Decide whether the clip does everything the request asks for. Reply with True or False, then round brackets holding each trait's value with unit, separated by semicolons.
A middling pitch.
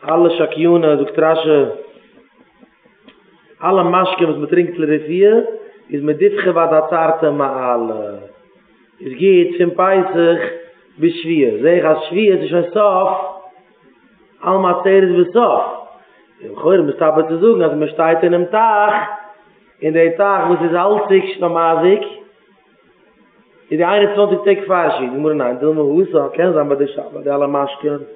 True (175 Hz)